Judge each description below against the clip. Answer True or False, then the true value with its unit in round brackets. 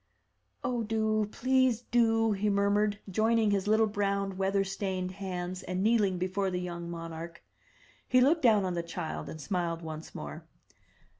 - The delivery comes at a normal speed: True (155 wpm)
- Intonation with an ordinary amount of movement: True (3.3 semitones)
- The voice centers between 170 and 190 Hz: False (200 Hz)